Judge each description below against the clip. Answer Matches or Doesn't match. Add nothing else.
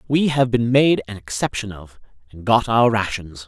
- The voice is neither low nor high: Doesn't match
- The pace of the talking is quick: Doesn't match